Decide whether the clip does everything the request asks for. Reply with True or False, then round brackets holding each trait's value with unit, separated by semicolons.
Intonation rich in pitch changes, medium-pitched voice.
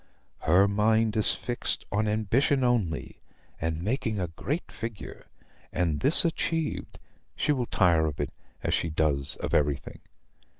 False (7.0 semitones; 105 Hz)